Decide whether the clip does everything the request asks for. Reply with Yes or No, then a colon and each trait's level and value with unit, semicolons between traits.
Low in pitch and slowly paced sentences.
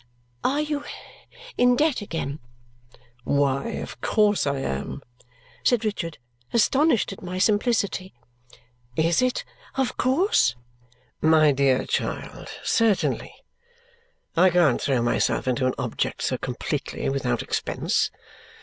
No: medium, 180 Hz; slow, 115 wpm